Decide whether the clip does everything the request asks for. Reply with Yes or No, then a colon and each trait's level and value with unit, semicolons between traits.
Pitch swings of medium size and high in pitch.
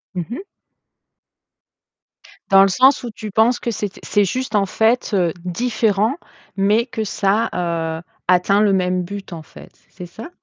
Yes: average, 3.6 semitones; high, 200 Hz